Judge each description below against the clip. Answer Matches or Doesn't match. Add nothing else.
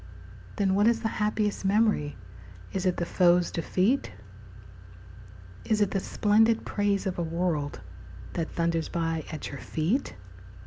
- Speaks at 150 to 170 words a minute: Doesn't match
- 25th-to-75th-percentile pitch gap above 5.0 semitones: Doesn't match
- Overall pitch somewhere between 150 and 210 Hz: Matches